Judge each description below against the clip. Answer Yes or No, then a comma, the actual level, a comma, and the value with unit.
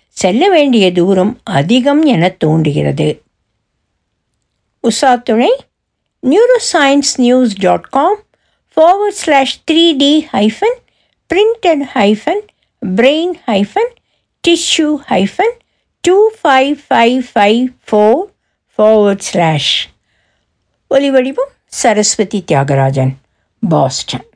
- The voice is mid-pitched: No, very high, 255 Hz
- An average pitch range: No, wide, 8.7 semitones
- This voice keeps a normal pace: Yes, average, 85 wpm